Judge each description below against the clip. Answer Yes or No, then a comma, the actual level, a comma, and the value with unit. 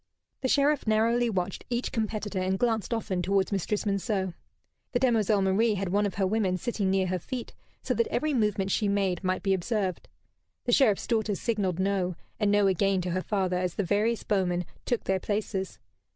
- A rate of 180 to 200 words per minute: Yes, average, 190 wpm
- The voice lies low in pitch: No, high, 200 Hz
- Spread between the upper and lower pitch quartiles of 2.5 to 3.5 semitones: Yes, average, 2.9 semitones